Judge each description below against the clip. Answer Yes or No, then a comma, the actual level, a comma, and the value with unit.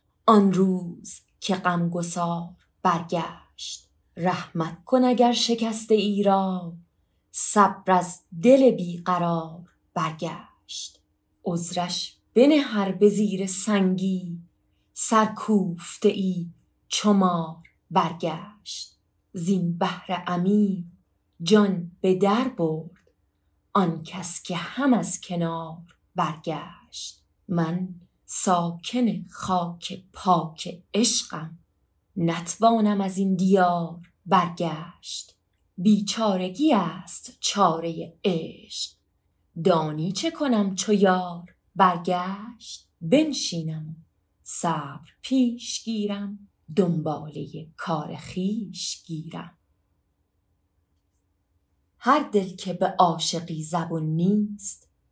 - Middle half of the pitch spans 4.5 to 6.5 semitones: No, average, 3.6 semitones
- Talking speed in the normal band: No, slow, 85 wpm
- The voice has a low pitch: No, medium, 180 Hz